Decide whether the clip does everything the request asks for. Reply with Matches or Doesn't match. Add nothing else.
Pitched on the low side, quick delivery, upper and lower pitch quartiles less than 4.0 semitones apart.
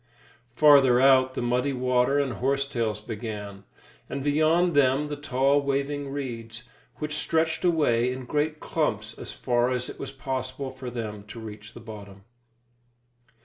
Doesn't match